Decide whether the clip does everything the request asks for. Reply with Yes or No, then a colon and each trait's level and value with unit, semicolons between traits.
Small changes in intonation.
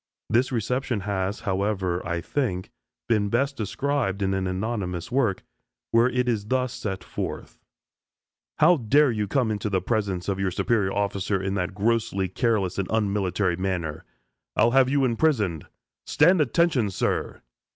No: average, 4.4 semitones